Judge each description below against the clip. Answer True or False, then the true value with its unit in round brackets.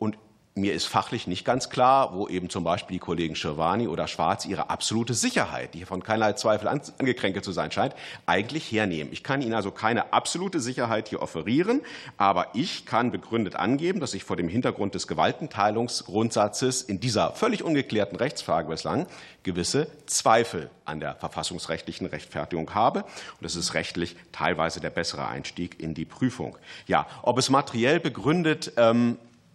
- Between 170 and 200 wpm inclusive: False (160 wpm)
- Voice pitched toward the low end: True (105 Hz)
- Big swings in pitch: True (5.9 semitones)